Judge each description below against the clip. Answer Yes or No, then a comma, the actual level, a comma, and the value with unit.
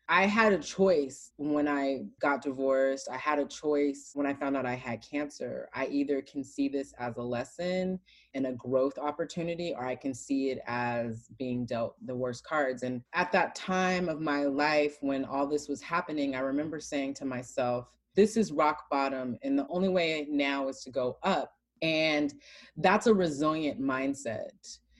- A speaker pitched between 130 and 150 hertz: Yes, medium, 140 Hz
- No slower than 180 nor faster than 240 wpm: Yes, average, 185 wpm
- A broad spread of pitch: No, average, 3.0 semitones